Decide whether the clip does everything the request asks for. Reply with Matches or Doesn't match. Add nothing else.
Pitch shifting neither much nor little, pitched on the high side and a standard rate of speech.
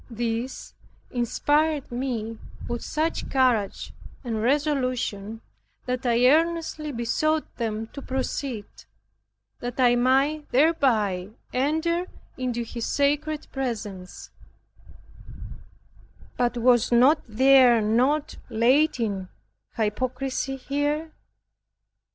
Doesn't match